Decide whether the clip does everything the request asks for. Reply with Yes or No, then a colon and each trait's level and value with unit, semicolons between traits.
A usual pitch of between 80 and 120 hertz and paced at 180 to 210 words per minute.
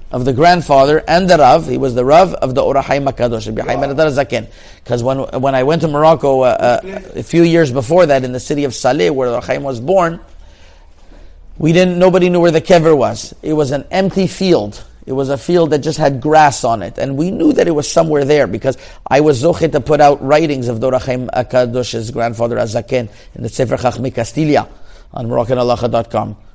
No: low, 135 Hz; average, 200 wpm